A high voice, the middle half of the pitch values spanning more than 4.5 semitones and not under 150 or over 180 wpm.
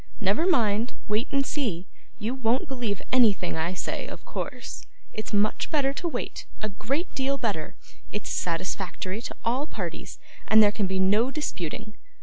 Yes: high, 220 Hz; average, 5.0 semitones; average, 160 wpm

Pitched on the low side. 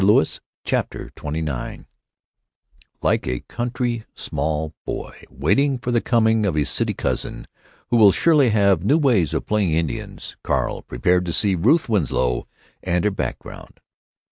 Yes: low, 100 Hz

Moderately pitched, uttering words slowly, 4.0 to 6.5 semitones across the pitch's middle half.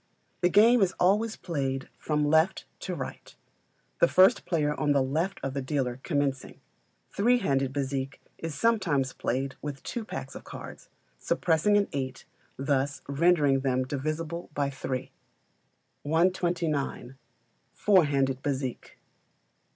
Yes: medium, 145 Hz; slow, 130 wpm; average, 4.5 semitones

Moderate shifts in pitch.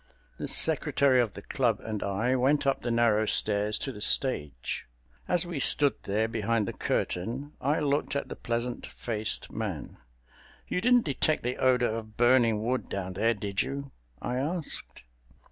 Yes: average, 4.3 semitones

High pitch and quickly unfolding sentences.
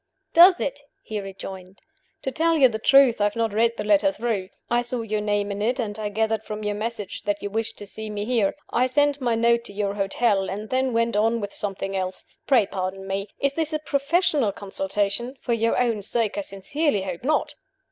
Yes: high, 220 Hz; fast, 220 wpm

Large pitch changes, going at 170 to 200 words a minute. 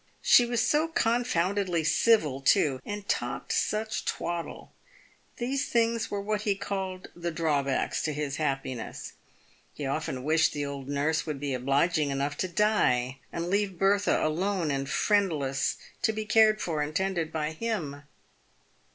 No: wide, 6.3 semitones; average, 150 wpm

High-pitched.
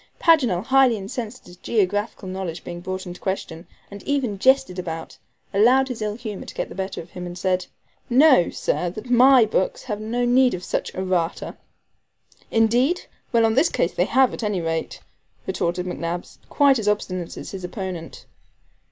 Yes: high, 205 Hz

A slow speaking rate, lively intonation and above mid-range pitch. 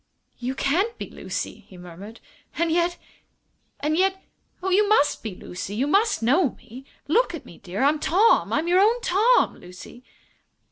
No: average, 170 wpm; wide, 8.5 semitones; very high, 320 Hz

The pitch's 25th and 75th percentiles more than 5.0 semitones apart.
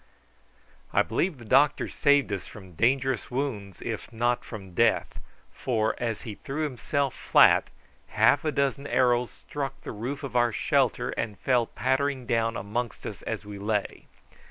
No: average, 4.1 semitones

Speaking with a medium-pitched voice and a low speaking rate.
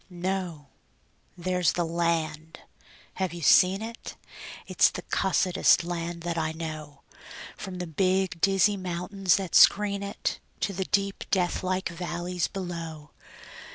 Yes: medium, 180 Hz; slow, 125 wpm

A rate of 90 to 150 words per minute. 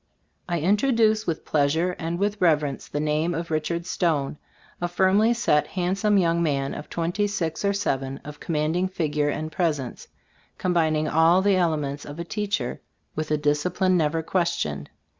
No: average, 170 wpm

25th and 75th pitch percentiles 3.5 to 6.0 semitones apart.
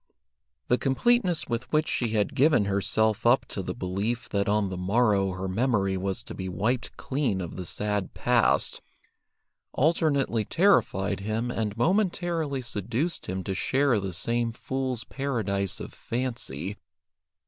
Yes: average, 5.2 semitones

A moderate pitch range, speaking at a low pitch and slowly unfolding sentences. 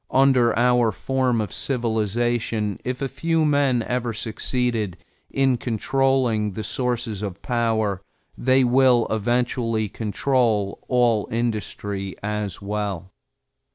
Yes: average, 3.1 semitones; low, 115 Hz; slow, 110 wpm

